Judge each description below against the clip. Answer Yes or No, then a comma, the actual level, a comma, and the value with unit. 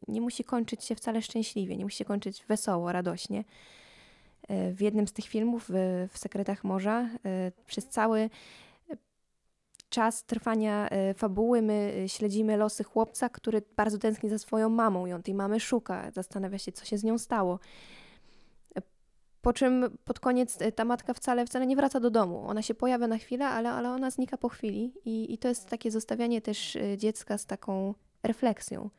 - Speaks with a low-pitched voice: No, high, 220 Hz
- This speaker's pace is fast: Yes, fast, 165 wpm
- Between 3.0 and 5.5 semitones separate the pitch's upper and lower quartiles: No, narrow, 2.6 semitones